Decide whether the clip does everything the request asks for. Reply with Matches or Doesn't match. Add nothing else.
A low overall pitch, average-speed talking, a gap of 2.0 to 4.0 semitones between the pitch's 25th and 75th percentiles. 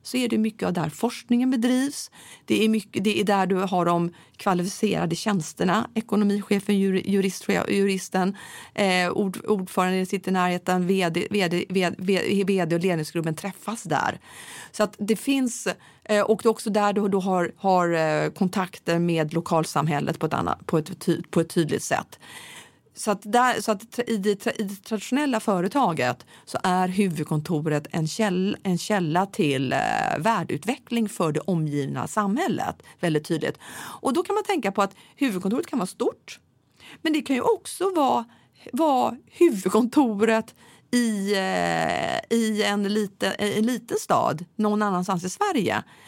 Doesn't match